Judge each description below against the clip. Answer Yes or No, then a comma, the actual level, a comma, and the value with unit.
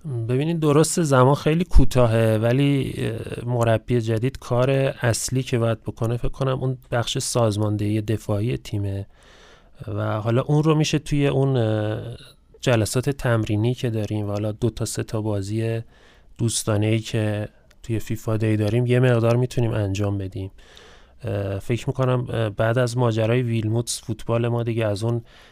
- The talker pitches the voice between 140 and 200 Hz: No, low, 115 Hz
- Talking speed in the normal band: Yes, average, 140 wpm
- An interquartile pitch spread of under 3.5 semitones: Yes, average, 2.8 semitones